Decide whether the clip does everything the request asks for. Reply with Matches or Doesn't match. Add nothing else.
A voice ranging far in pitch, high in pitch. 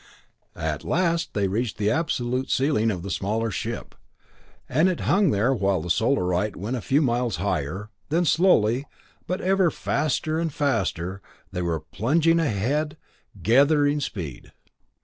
Doesn't match